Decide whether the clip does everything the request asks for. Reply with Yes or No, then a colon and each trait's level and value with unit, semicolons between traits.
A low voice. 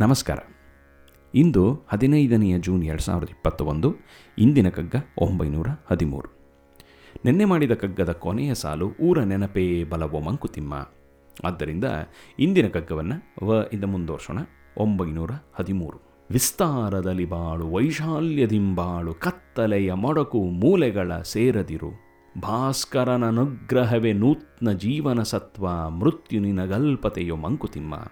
Yes: very low, 95 Hz